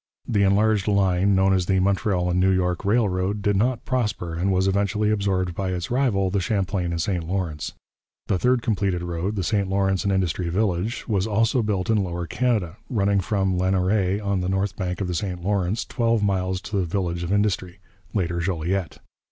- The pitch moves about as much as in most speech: No, narrow, 2.2 semitones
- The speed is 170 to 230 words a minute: Yes, average, 195 wpm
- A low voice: Yes, very low, 95 Hz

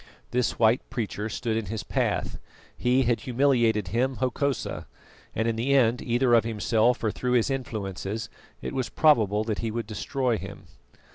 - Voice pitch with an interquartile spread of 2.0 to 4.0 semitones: Yes, narrow, 2.5 semitones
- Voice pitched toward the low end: Yes, low, 115 Hz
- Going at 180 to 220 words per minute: No, average, 165 wpm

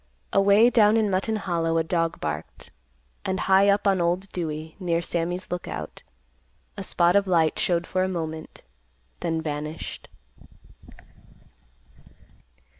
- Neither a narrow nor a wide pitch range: Yes, average, 3.0 semitones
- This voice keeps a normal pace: No, slow, 125 wpm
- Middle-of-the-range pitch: Yes, medium, 175 Hz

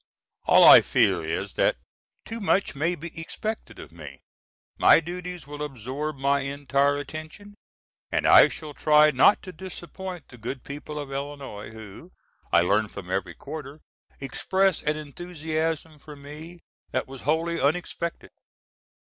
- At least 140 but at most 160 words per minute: Yes, average, 145 wpm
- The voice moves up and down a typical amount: Yes, average, 3.6 semitones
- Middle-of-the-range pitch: Yes, medium, 150 Hz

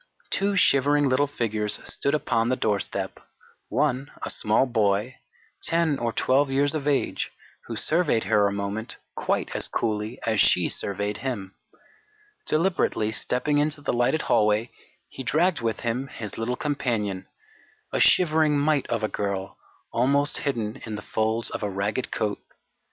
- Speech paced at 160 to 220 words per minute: No, average, 150 wpm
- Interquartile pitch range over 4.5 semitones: Yes, average, 5.1 semitones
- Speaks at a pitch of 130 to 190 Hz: No, low, 120 Hz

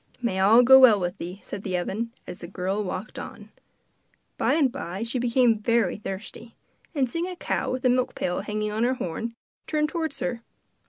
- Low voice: No, high, 230 Hz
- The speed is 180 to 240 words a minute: Yes, average, 200 wpm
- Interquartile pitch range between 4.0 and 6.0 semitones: Yes, average, 4.7 semitones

